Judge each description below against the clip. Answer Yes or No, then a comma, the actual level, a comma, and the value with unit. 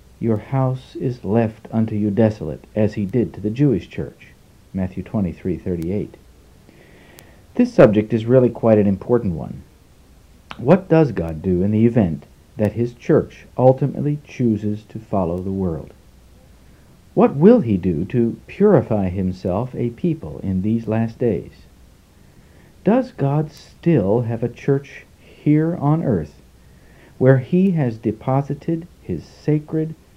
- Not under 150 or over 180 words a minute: No, slow, 135 wpm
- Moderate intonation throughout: No, wide, 6.4 semitones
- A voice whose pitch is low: Yes, low, 110 Hz